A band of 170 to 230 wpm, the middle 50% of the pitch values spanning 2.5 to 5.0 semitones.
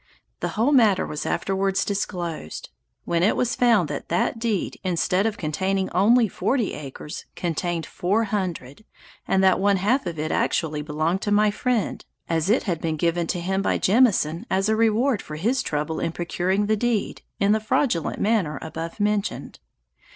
Yes: average, 175 wpm; average, 4.4 semitones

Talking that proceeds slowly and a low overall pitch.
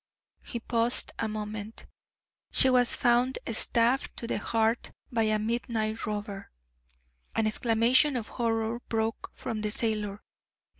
No: slow, 130 wpm; high, 225 Hz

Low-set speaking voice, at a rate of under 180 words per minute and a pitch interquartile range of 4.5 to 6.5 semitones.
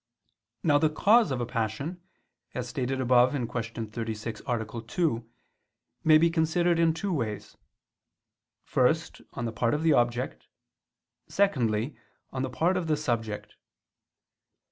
Yes: low, 130 Hz; slow, 135 wpm; wide, 5.6 semitones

